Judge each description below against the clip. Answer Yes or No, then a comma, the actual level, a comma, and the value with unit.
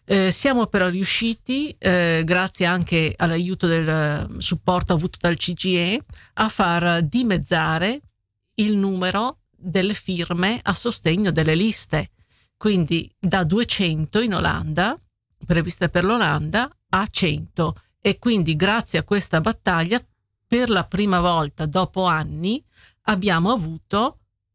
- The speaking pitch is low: No, medium, 185 Hz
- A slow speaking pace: Yes, slow, 115 wpm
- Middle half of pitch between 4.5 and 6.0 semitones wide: No, average, 3.7 semitones